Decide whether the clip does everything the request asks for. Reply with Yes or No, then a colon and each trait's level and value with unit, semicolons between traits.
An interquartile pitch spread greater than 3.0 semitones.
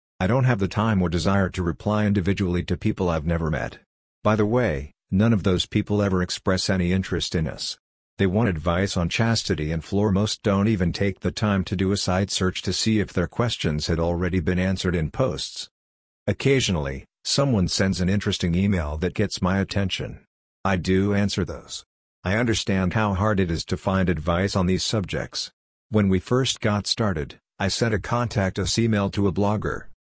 No: narrow, 2.6 semitones